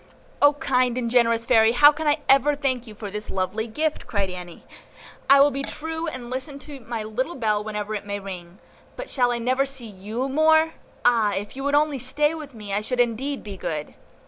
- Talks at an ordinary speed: No, fast, 215 wpm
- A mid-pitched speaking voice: No, high, 245 Hz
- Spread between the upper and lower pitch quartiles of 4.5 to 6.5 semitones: Yes, average, 5.0 semitones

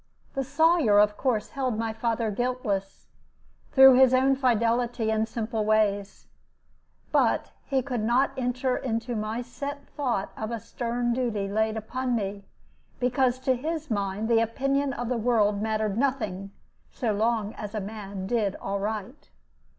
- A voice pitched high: Yes, high, 230 Hz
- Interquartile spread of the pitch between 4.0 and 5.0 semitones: No, average, 3.2 semitones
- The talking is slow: No, average, 150 wpm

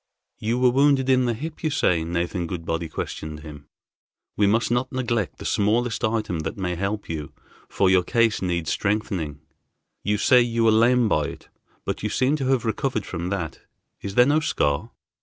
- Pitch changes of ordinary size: No, wide, 6.0 semitones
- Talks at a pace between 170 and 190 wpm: Yes, average, 185 wpm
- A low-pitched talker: Yes, low, 105 Hz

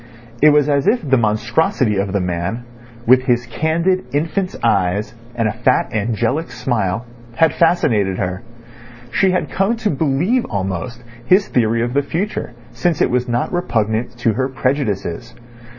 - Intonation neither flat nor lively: No, wide, 6.6 semitones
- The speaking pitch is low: Yes, low, 125 Hz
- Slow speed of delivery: No, average, 155 wpm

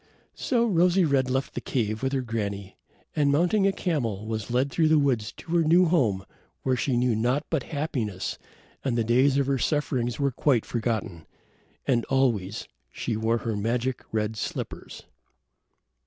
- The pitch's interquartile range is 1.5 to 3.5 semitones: No, average, 4.6 semitones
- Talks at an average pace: Yes, average, 170 wpm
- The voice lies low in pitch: Yes, low, 125 Hz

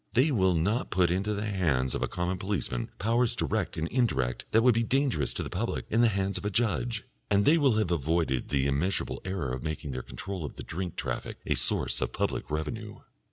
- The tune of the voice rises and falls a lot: Yes, wide, 6.1 semitones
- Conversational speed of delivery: No, fast, 220 wpm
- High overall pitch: No, very low, 95 Hz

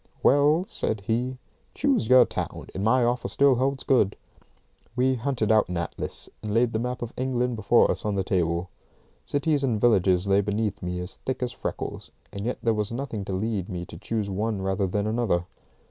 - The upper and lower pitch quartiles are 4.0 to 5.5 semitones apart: Yes, average, 4.3 semitones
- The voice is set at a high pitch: No, low, 110 Hz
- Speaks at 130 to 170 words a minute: No, average, 195 wpm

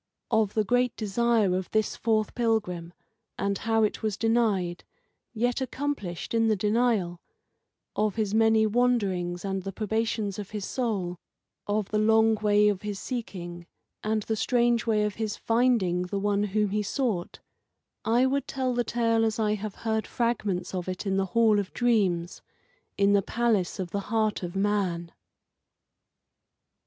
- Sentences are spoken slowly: No, average, 160 wpm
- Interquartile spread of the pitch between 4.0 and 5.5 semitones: No, average, 2.8 semitones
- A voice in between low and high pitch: No, high, 215 Hz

